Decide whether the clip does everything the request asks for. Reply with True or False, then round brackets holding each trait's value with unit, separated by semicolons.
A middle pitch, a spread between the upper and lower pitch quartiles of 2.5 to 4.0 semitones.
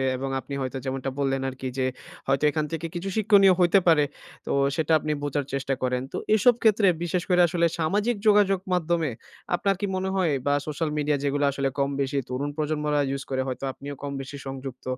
False (150 Hz; 4.7 semitones)